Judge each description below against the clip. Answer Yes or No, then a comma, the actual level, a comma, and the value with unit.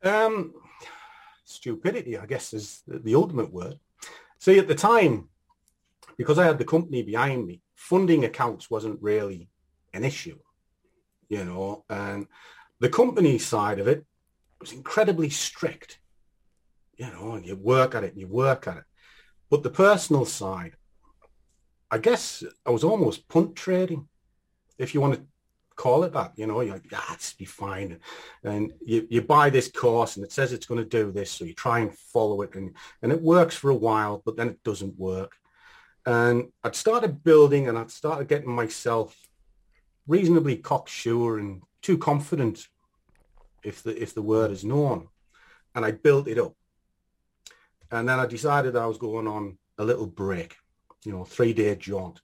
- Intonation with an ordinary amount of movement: No, wide, 6.6 semitones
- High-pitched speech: No, low, 115 Hz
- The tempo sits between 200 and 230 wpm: No, average, 170 wpm